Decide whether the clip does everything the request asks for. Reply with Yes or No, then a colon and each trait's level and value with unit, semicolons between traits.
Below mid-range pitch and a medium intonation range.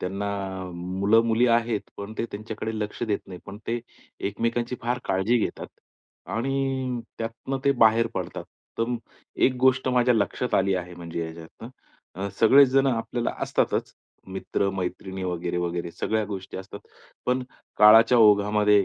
Yes: low, 110 Hz; average, 3.8 semitones